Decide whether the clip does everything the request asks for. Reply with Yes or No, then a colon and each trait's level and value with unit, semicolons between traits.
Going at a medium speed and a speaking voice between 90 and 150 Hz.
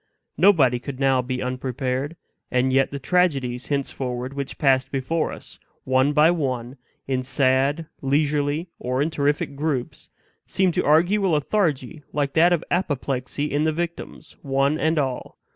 Yes: average, 150 wpm; medium, 140 Hz